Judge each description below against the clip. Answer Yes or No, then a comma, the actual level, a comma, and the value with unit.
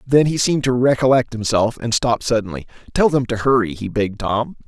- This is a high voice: No, low, 120 Hz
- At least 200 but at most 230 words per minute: Yes, fast, 205 wpm